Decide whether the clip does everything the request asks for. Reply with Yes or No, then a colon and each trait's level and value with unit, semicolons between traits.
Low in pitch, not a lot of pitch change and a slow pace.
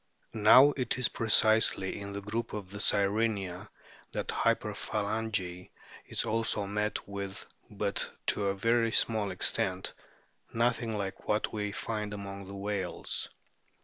Yes: low, 105 Hz; narrow, 2.1 semitones; slow, 130 wpm